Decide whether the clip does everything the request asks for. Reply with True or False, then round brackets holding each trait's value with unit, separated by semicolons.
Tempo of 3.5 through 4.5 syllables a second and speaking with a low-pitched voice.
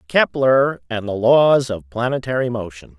True (4.4 syllables/s; 120 Hz)